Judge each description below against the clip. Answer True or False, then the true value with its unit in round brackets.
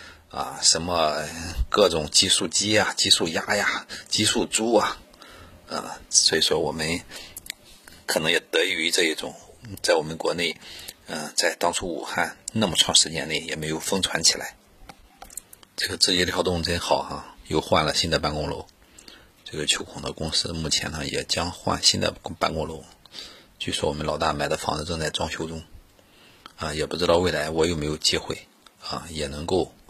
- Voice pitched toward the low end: True (80 Hz)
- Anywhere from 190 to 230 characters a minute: False (255 characters per minute)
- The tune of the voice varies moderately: False (1.9 semitones)